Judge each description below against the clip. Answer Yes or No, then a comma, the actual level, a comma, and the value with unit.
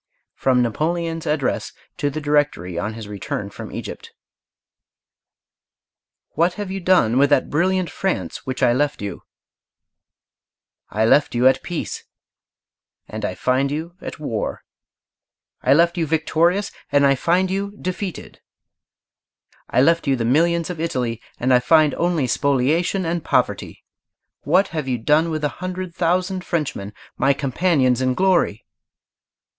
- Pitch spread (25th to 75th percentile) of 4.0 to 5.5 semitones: Yes, average, 5.1 semitones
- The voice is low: No, medium, 150 Hz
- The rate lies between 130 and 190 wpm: Yes, average, 140 wpm